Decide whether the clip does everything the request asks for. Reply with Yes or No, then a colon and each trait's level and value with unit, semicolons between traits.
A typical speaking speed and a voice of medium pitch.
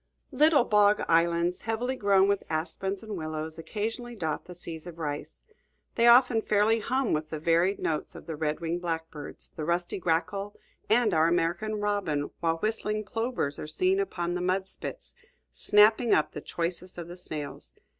Yes: average, 170 wpm; medium, 180 Hz